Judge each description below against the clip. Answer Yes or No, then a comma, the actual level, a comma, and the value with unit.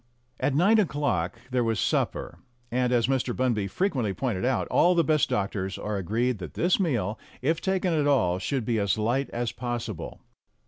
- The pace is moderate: Yes, average, 180 wpm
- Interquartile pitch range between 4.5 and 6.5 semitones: Yes, wide, 5.5 semitones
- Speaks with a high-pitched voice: No, low, 120 Hz